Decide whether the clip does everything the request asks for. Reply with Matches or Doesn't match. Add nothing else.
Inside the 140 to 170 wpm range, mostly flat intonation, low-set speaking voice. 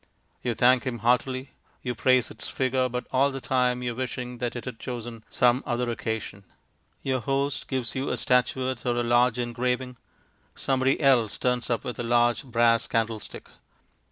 Doesn't match